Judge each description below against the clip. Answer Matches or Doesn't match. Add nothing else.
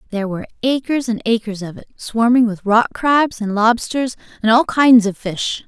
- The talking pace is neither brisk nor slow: Matches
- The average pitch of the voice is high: Matches